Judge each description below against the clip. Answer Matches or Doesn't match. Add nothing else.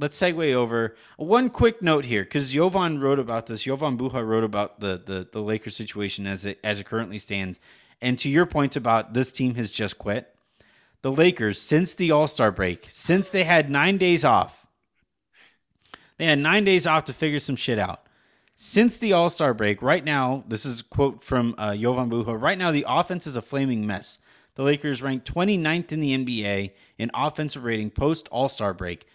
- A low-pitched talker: Matches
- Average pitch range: Doesn't match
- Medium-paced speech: Matches